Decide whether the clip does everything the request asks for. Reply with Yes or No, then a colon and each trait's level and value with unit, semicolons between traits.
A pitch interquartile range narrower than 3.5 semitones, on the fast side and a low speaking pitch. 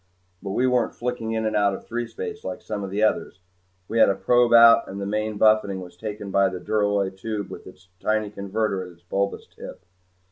Yes: narrow, 2.4 semitones; fast, 215 wpm; low, 105 Hz